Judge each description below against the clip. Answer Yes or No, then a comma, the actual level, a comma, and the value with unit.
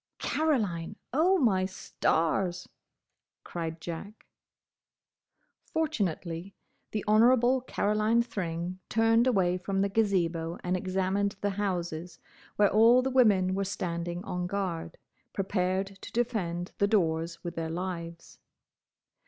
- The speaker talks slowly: Yes, slow, 110 wpm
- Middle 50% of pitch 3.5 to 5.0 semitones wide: Yes, average, 3.8 semitones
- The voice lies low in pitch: No, high, 190 Hz